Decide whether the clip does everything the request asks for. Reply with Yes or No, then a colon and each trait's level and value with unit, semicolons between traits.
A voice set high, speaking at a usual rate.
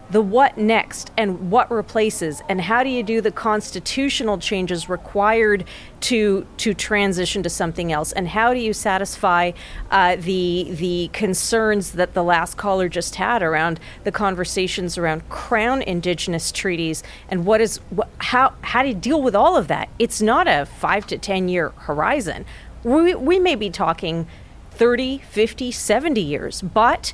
Yes: high, 200 Hz; average, 165 wpm